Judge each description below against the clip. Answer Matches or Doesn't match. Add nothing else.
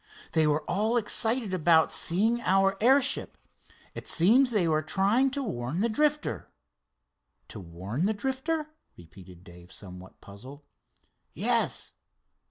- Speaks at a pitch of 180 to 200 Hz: Matches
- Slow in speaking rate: Matches